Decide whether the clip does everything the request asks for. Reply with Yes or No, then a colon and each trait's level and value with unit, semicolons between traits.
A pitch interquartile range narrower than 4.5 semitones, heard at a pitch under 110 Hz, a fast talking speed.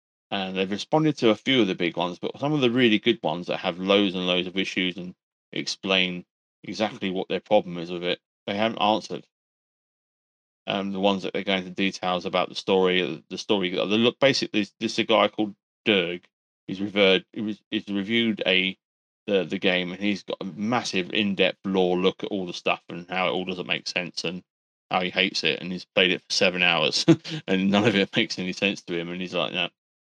Yes: average, 2.7 semitones; very low, 95 Hz; fast, 220 wpm